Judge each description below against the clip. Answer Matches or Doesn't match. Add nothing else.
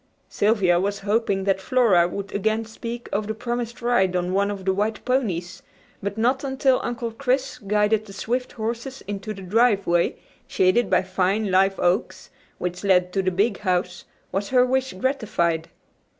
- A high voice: Matches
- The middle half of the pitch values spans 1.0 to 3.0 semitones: Doesn't match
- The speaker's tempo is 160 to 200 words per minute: Matches